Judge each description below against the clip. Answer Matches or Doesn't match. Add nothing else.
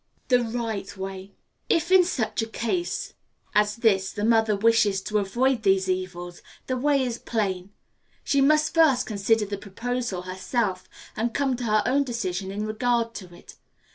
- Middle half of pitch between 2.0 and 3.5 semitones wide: Doesn't match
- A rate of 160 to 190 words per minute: Matches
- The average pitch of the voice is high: Matches